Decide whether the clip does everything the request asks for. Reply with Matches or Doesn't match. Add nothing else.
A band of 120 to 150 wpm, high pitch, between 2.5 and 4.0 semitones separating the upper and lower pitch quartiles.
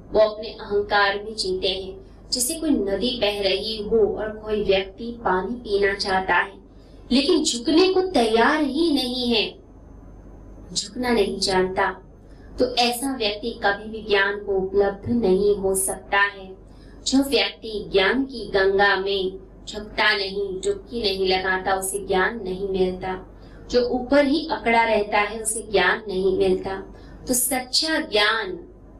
Matches